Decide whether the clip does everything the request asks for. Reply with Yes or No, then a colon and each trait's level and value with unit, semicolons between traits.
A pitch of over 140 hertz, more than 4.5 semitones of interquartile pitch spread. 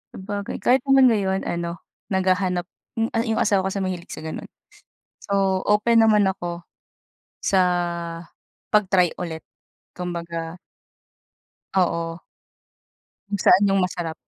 No: high, 190 Hz; average, 2.8 semitones